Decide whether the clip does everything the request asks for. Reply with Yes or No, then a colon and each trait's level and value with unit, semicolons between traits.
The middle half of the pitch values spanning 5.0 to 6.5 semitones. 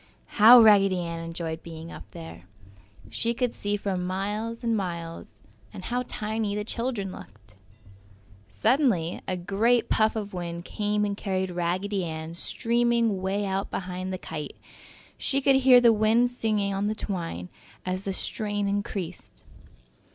No: average, 4.1 semitones